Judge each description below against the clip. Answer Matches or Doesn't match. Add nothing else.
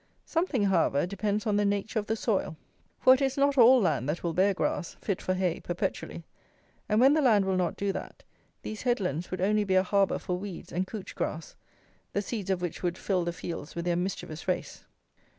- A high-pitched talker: Matches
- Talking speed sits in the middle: Doesn't match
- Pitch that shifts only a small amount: Doesn't match